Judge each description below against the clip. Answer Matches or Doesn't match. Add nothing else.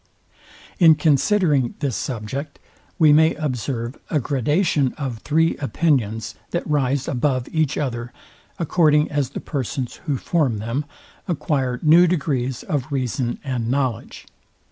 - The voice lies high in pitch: Doesn't match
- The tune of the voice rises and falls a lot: Doesn't match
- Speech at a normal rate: Doesn't match